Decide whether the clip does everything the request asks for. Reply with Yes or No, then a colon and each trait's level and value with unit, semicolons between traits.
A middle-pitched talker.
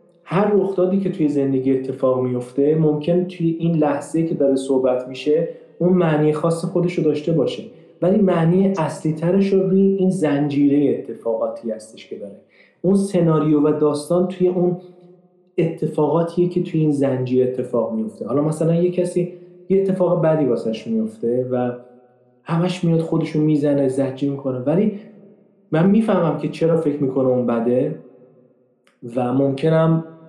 Yes: medium, 160 Hz